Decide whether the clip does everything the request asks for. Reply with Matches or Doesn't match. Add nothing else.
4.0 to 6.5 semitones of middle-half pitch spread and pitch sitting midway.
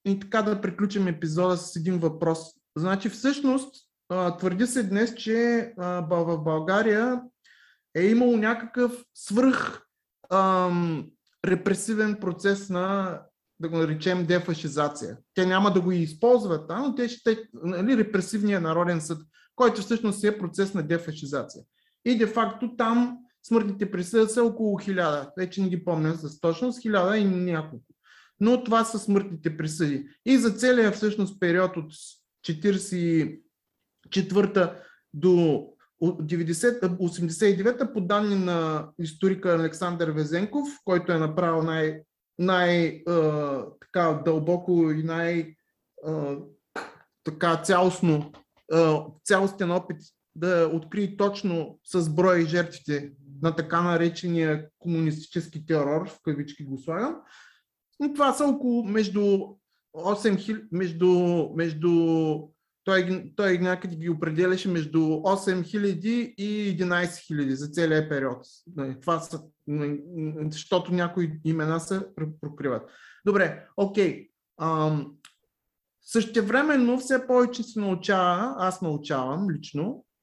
Matches